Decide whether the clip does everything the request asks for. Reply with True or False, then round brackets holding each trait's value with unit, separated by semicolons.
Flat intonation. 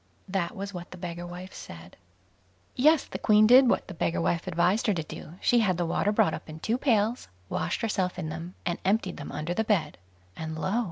False (4.1 semitones)